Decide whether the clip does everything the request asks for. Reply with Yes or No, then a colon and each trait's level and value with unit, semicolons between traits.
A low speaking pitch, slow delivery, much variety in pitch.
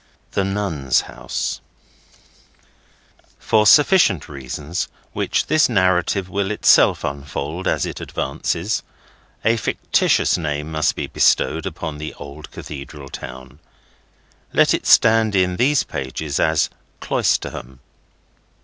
Yes: very low, 80 Hz; slow, 110 wpm; wide, 5.8 semitones